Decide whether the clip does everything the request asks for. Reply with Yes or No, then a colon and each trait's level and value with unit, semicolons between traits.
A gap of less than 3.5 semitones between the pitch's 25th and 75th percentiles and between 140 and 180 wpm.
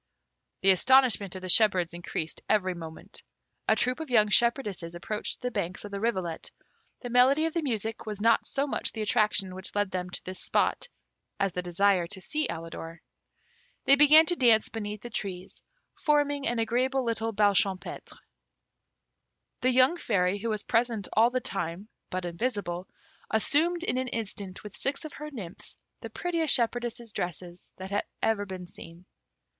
No: average, 5.2 semitones; average, 170 wpm